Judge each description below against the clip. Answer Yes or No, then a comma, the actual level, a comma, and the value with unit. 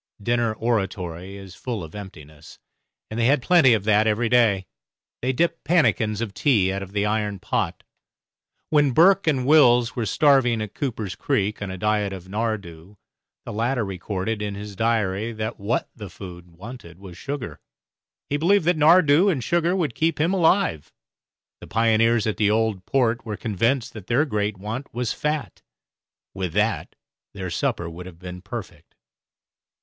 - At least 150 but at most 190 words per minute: Yes, average, 165 wpm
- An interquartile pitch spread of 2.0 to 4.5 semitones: No, average, 4.9 semitones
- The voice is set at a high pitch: No, low, 110 Hz